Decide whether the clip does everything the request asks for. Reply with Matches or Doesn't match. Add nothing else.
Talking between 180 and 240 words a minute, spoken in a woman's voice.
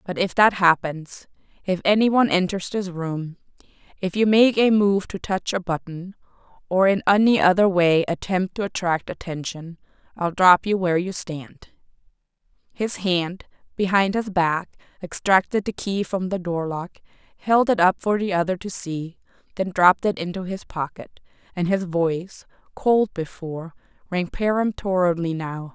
Doesn't match